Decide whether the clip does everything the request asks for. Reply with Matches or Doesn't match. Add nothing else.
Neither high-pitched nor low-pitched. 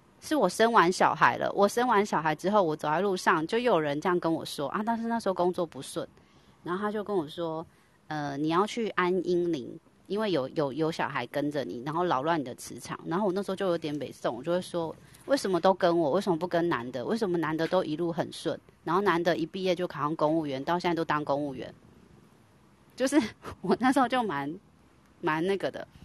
Matches